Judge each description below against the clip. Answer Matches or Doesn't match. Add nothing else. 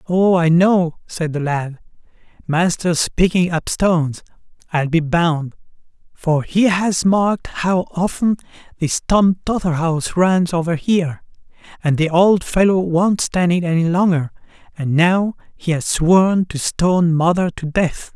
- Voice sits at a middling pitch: Matches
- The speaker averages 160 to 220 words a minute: Doesn't match